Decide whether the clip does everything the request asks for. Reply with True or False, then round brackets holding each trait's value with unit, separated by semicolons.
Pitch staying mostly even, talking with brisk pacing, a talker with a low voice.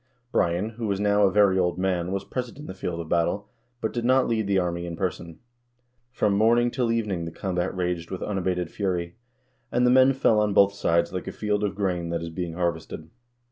False (3.5 semitones; 220 wpm; 95 Hz)